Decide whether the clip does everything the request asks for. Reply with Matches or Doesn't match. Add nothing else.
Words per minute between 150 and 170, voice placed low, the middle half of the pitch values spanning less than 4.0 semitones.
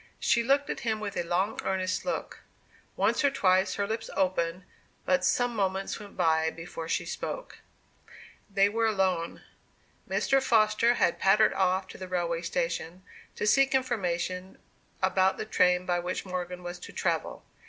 Doesn't match